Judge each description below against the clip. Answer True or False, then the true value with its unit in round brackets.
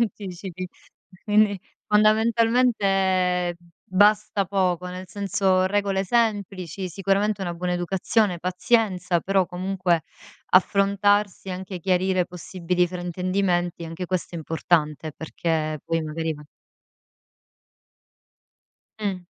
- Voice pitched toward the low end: False (185 Hz)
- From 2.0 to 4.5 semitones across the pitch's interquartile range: True (2.3 semitones)